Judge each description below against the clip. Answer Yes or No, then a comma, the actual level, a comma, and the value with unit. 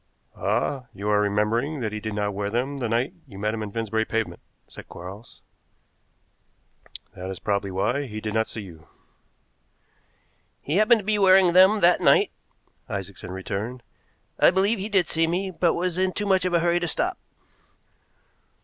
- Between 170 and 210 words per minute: Yes, average, 175 wpm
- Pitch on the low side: Yes, low, 120 Hz